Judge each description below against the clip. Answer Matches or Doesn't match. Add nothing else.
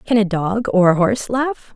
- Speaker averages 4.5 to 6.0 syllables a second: Matches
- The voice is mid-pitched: Doesn't match